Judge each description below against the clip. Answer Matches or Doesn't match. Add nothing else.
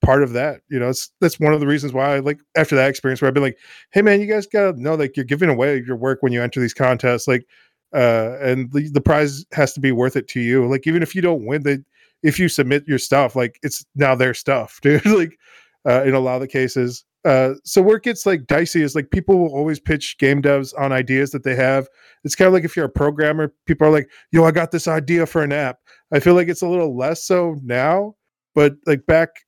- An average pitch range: Matches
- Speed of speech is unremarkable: Doesn't match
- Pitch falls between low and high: Matches